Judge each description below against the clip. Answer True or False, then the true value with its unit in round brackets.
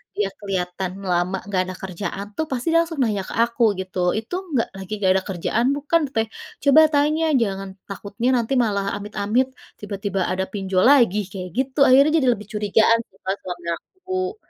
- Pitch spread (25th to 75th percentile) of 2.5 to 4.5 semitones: False (5.3 semitones)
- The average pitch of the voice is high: True (210 Hz)